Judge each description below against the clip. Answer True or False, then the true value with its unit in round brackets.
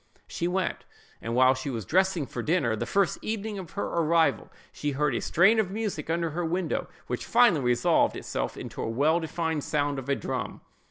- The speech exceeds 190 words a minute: True (200 wpm)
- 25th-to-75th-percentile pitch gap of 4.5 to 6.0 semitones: True (5.4 semitones)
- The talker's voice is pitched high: False (160 Hz)